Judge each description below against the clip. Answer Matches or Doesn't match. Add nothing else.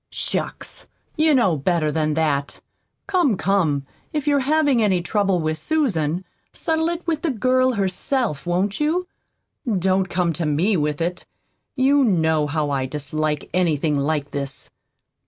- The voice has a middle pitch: Matches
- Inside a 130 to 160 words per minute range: Matches